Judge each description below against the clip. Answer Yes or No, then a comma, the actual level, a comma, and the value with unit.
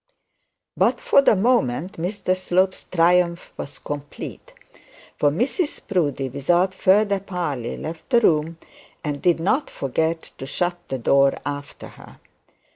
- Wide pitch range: No, average, 4.8 semitones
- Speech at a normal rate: No, slow, 130 wpm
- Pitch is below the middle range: No, medium, 170 Hz